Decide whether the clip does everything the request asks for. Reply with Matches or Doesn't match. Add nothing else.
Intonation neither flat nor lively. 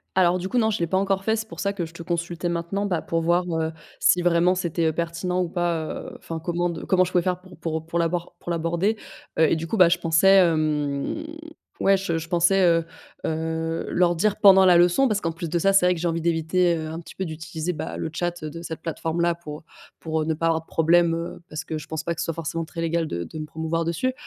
Doesn't match